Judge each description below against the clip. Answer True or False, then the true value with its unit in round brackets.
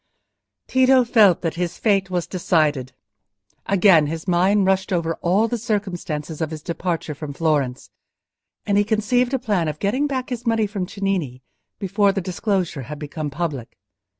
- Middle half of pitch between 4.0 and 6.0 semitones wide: True (4.7 semitones)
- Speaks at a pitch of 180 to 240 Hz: True (185 Hz)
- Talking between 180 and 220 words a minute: False (160 wpm)